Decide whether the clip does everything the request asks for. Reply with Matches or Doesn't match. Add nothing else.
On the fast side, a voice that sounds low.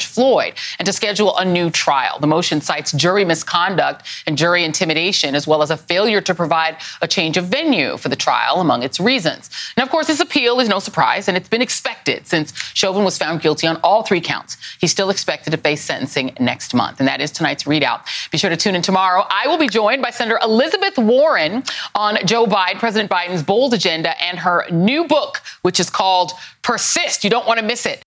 Doesn't match